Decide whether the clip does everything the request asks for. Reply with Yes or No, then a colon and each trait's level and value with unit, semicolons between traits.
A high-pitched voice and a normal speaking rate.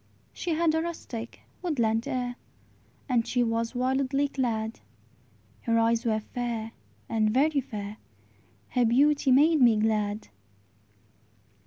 No: high, 245 Hz; slow, 120 wpm